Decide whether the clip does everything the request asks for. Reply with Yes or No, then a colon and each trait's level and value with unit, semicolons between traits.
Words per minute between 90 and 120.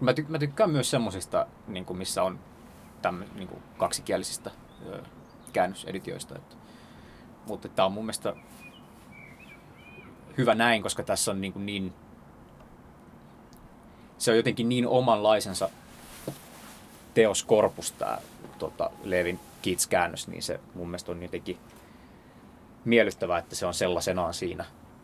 Yes: average, 100 wpm